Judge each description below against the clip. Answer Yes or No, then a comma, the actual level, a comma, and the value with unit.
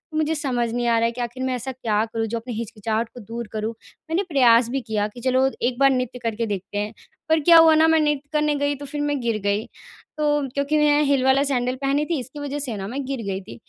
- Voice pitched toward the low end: No, very high, 255 Hz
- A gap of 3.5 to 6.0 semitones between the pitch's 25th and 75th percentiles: Yes, average, 4.0 semitones